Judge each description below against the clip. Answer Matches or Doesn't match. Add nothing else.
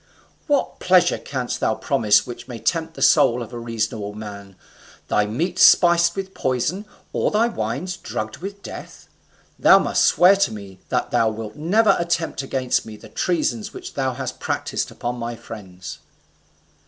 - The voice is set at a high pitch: Doesn't match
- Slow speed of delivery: Doesn't match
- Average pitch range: Doesn't match